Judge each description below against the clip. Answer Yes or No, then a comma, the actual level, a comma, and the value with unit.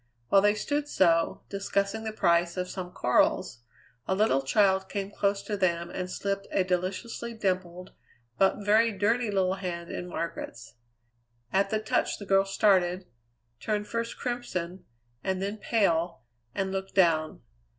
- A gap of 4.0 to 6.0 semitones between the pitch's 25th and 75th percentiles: No, narrow, 2.5 semitones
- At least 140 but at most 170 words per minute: Yes, average, 150 wpm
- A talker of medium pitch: No, high, 195 Hz